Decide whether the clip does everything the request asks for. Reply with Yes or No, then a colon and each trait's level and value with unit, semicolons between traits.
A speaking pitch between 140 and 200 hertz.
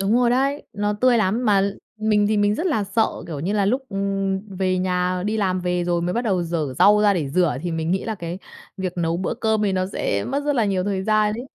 Yes: high, 195 Hz